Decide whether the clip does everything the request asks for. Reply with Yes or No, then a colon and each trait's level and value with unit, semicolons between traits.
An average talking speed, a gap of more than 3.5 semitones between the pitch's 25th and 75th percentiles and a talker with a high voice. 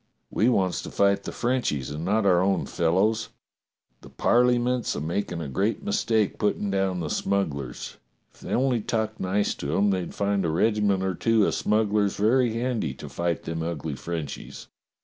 No: average, 175 wpm; average, 4.6 semitones; low, 100 Hz